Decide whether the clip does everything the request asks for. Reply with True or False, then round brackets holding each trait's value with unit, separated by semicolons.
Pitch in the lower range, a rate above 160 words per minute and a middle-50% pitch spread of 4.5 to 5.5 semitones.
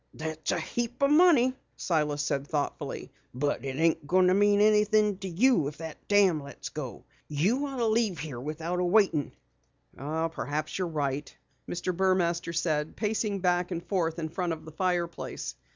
False (170 Hz; 170 wpm; 4.8 semitones)